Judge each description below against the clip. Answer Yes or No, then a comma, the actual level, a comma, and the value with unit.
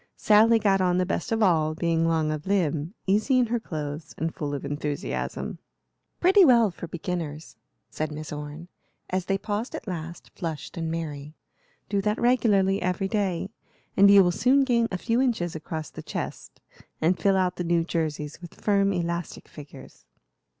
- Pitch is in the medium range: Yes, medium, 175 Hz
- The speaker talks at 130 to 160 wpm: No, average, 175 wpm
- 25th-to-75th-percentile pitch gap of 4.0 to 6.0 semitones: Yes, average, 4.4 semitones